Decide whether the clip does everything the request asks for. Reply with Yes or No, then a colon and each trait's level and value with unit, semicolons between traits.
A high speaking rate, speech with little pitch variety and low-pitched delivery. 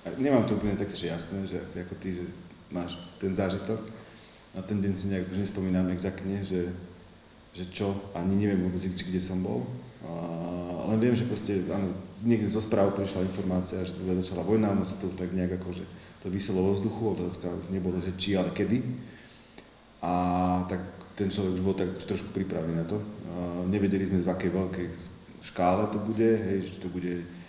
Yes: fast, 200 wpm; narrow, 1.7 semitones; very low, 95 Hz